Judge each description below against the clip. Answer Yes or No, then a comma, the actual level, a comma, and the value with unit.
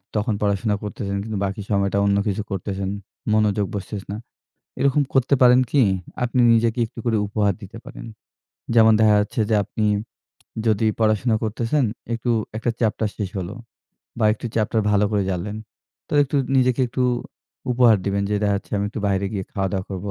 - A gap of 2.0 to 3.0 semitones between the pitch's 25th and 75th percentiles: Yes, narrow, 2.5 semitones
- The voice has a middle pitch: No, low, 105 Hz